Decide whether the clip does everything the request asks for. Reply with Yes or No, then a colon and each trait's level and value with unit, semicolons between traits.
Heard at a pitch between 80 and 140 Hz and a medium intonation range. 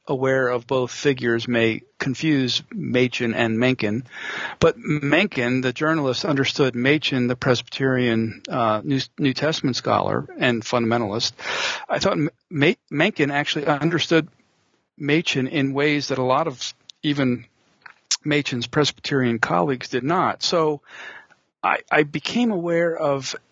Yes: low, 135 Hz; average, 3.3 semitones